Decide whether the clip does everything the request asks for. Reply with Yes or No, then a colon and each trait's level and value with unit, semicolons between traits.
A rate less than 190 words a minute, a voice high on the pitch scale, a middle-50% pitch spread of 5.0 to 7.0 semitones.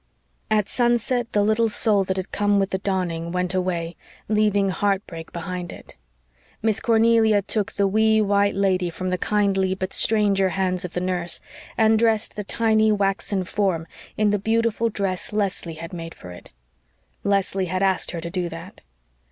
No: average, 170 wpm; high, 195 Hz; average, 2.7 semitones